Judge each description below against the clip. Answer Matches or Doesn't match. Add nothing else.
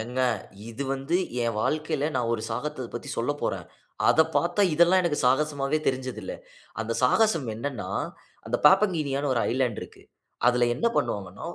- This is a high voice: Doesn't match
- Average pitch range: Matches